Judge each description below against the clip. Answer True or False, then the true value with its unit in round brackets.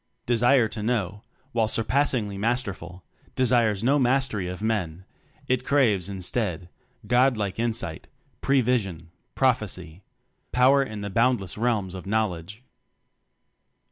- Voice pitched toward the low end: True (110 Hz)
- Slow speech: True (125 wpm)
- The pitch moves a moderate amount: True (4.5 semitones)